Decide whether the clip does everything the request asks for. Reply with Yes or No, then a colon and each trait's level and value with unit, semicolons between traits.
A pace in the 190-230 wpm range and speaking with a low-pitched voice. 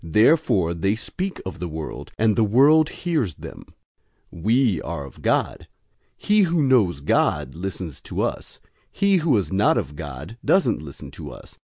No: average, 170 wpm; low, 105 Hz